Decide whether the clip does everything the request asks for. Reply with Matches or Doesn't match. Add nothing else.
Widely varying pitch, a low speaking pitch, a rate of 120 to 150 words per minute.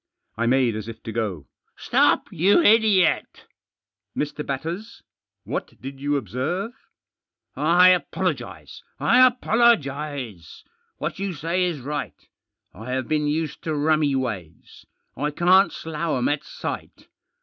Doesn't match